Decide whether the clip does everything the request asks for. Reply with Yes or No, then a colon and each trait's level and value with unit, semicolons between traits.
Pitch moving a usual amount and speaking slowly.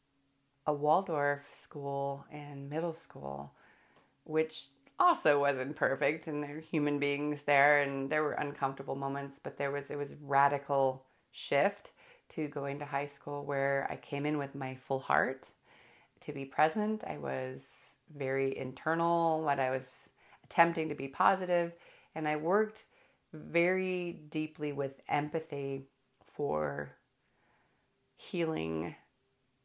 No: narrow, 2.2 semitones; slow, 130 wpm